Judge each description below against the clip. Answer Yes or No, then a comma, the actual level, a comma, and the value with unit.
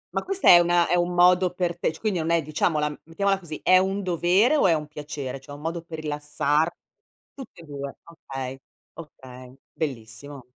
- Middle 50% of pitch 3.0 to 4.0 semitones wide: Yes, average, 3.5 semitones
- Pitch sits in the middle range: Yes, medium, 160 Hz